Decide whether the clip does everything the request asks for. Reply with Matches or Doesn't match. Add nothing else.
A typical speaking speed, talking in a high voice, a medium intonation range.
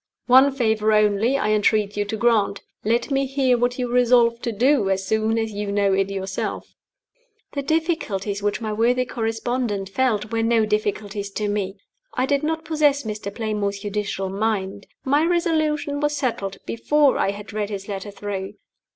Matches